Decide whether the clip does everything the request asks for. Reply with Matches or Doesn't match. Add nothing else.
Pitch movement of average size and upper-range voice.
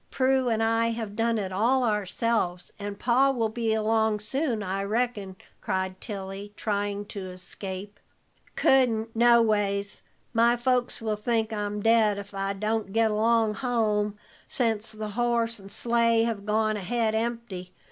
Doesn't match